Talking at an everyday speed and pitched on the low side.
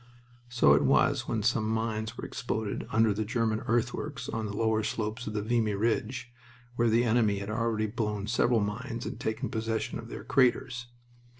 Yes: average, 180 wpm; low, 110 Hz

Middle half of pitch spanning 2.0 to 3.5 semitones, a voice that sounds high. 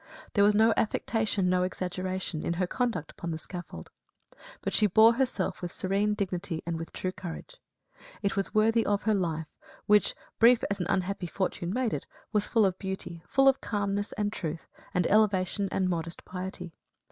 Yes: average, 2.9 semitones; high, 195 Hz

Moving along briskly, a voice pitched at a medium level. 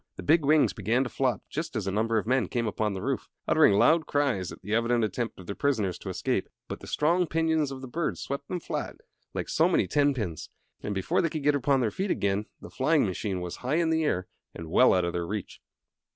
No: fast, 245 wpm; low, 120 Hz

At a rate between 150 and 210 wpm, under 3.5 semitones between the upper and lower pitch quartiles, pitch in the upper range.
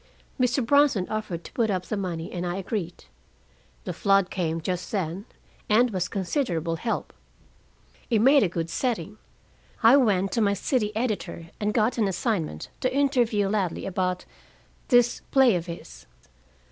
No: average, 155 wpm; average, 4.8 semitones; high, 200 Hz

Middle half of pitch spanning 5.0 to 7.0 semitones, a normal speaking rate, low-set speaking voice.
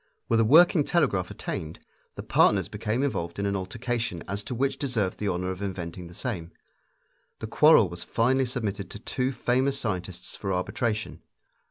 Yes: wide, 5.4 semitones; average, 170 wpm; low, 105 Hz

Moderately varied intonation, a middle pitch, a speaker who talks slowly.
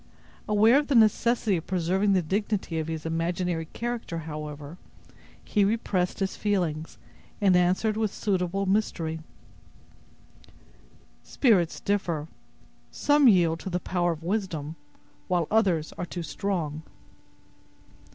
Yes: average, 4.1 semitones; medium, 180 Hz; slow, 120 wpm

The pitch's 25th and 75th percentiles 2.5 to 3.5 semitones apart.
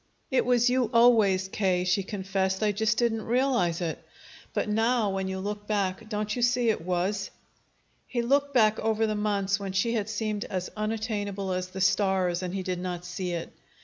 Yes: average, 2.9 semitones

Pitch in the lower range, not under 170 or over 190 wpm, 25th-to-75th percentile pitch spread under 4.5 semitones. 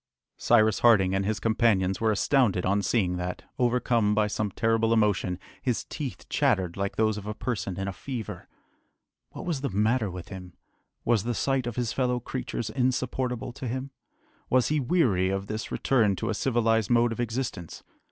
Yes: low, 115 Hz; average, 180 wpm; average, 3.9 semitones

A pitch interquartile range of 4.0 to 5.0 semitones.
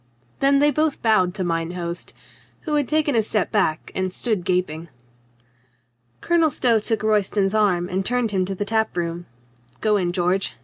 Yes: average, 4.5 semitones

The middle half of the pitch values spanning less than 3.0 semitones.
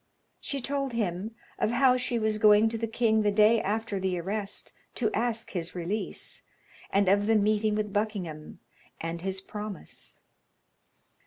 Yes: narrow, 2.4 semitones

